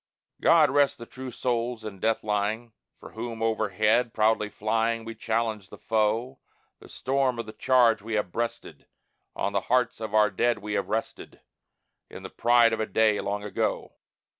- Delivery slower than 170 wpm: No, average, 175 wpm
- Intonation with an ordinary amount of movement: No, narrow, 1.9 semitones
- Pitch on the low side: Yes, low, 115 Hz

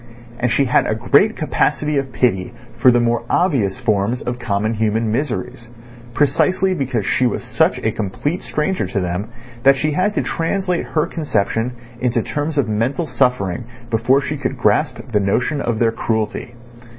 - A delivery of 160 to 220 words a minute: Yes, average, 170 wpm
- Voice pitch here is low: Yes, low, 125 Hz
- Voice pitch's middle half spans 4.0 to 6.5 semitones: Yes, average, 4.9 semitones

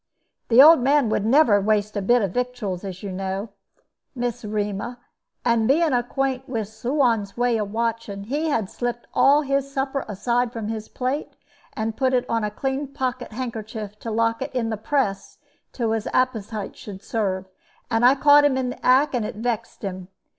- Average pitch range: Yes, average, 3.6 semitones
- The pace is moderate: Yes, average, 185 wpm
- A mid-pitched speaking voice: No, high, 235 Hz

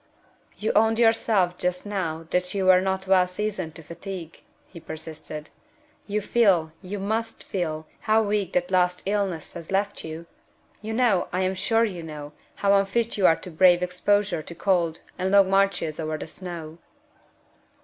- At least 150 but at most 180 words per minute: Yes, average, 170 wpm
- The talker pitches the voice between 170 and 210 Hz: Yes, medium, 185 Hz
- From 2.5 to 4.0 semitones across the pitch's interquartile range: Yes, average, 3.3 semitones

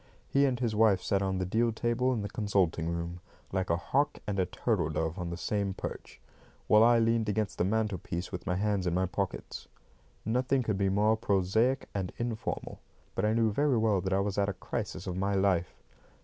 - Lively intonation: No, average, 3.2 semitones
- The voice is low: Yes, low, 100 Hz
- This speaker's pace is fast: Yes, fast, 210 wpm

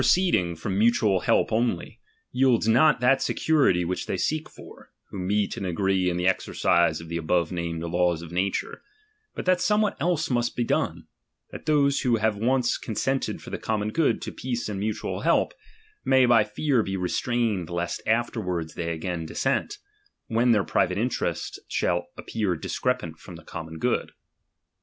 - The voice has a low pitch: Yes, low, 105 Hz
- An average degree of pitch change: No, wide, 6.0 semitones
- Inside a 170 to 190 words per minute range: Yes, average, 180 wpm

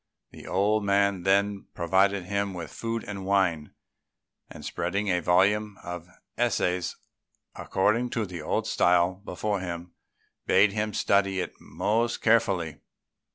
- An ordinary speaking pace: No, slow, 130 wpm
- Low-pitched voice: Yes, low, 100 Hz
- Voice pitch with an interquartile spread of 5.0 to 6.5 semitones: No, average, 2.8 semitones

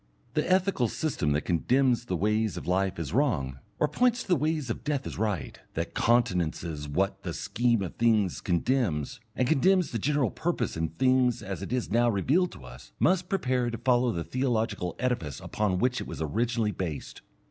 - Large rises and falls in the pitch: Yes, wide, 6.4 semitones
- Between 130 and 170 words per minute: No, average, 190 wpm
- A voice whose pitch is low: Yes, low, 115 Hz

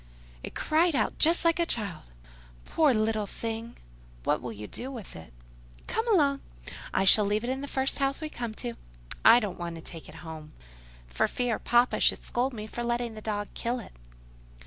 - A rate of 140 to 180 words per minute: No, average, 190 wpm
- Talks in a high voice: Yes, high, 235 Hz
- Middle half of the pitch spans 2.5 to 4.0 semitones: No, average, 4.6 semitones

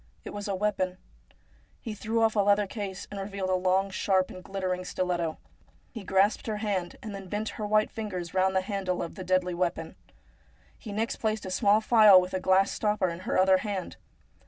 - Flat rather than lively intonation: Yes, narrow, 2.1 semitones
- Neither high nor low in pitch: No, high, 195 Hz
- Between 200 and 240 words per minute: Yes, fast, 205 wpm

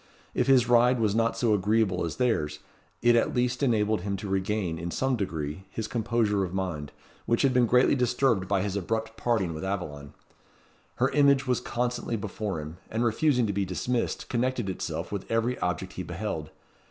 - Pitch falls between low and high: No, low, 110 Hz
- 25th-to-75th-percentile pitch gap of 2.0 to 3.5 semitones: No, average, 4.3 semitones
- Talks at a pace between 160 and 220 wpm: Yes, average, 185 wpm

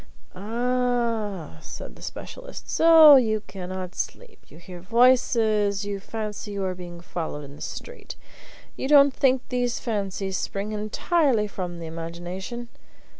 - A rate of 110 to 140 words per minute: Yes, slow, 135 wpm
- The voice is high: Yes, high, 210 Hz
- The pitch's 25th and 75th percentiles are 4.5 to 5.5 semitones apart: Yes, average, 5.1 semitones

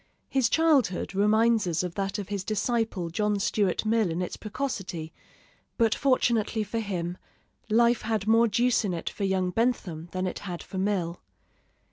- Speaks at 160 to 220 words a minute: Yes, average, 165 wpm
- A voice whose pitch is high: Yes, high, 205 Hz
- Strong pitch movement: No, average, 3.8 semitones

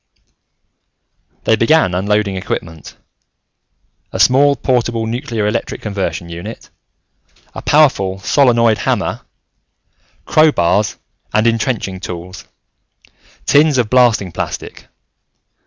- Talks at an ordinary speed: No, slow, 90 wpm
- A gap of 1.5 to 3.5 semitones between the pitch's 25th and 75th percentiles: No, average, 4.8 semitones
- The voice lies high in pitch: No, low, 110 Hz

